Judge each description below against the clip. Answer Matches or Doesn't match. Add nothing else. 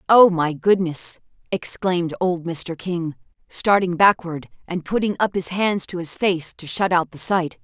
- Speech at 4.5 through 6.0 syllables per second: Doesn't match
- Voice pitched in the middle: Matches